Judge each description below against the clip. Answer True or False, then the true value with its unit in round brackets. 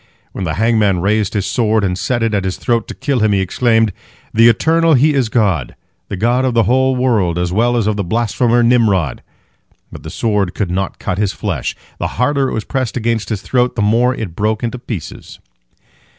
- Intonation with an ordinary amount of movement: True (3.6 semitones)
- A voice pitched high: False (110 Hz)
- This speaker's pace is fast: True (210 wpm)